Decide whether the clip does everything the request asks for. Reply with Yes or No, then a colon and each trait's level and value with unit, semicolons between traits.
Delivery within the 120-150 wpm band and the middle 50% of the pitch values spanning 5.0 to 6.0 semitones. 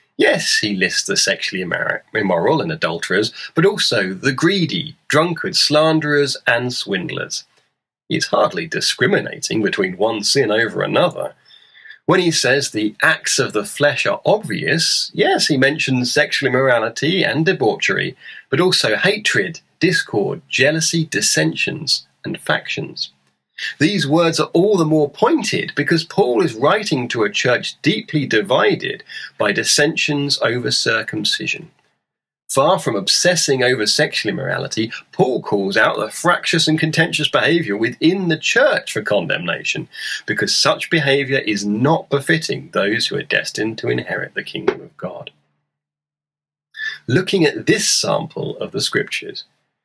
No: slow, 135 wpm; average, 4.5 semitones